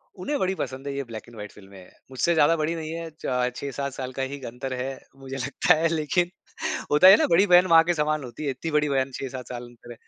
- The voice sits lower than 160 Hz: Yes, medium, 140 Hz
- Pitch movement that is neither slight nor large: Yes, average, 4.5 semitones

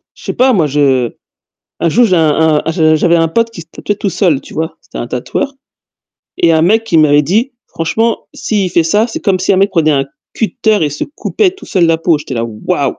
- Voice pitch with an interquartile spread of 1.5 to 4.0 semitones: No, wide, 5.5 semitones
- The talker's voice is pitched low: No, medium, 165 Hz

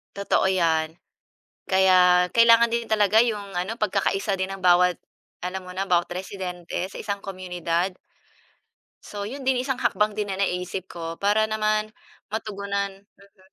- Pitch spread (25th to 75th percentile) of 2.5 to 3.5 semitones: Yes, average, 2.8 semitones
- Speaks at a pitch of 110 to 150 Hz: No, high, 195 Hz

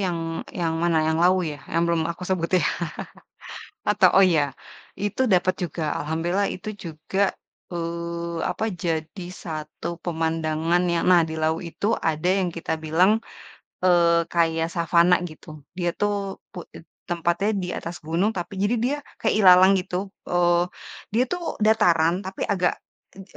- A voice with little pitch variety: Yes, narrow, 2.3 semitones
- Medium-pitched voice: Yes, medium, 175 Hz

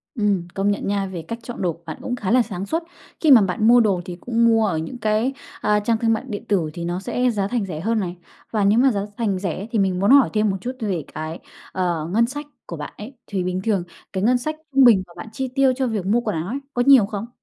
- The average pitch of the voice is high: Yes, high, 210 Hz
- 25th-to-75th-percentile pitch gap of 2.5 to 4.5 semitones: Yes, average, 4.2 semitones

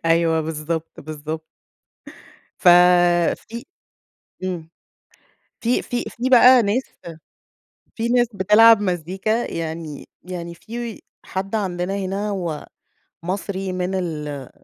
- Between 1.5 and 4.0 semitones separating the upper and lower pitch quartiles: No, average, 4.8 semitones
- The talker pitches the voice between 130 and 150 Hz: No, medium, 185 Hz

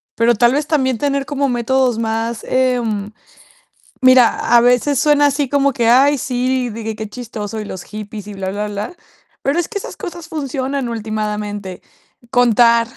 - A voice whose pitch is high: Yes, high, 240 Hz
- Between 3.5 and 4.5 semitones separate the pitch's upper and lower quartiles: Yes, average, 3.9 semitones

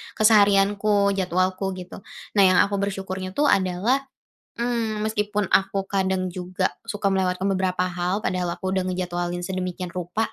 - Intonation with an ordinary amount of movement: No, narrow, 1.8 semitones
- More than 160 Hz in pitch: Yes, high, 190 Hz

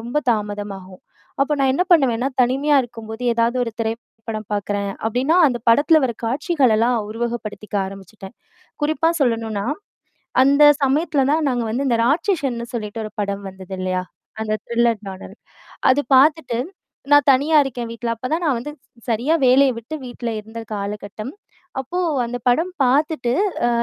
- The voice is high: Yes, high, 240 Hz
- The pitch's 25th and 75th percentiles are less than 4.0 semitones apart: No, average, 4.3 semitones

